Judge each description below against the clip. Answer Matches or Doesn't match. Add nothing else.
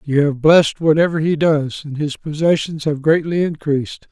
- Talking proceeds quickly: Doesn't match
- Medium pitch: Matches